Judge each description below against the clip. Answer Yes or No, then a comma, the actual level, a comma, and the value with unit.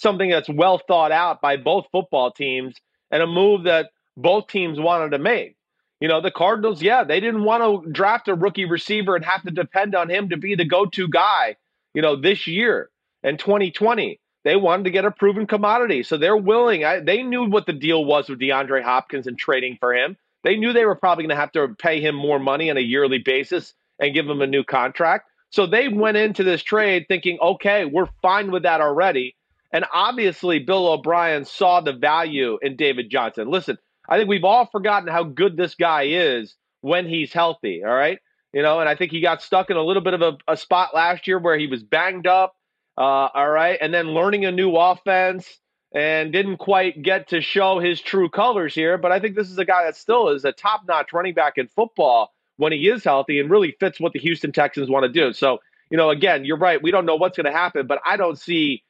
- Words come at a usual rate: No, fast, 230 wpm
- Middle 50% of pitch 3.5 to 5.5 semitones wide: Yes, average, 4.2 semitones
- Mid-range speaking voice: Yes, medium, 180 Hz